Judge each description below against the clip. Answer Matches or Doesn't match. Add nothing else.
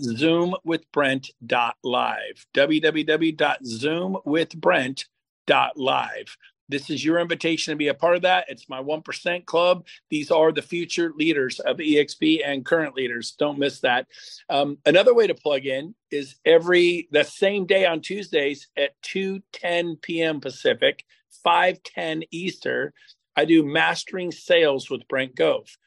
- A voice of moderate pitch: Matches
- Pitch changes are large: Doesn't match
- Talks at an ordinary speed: Doesn't match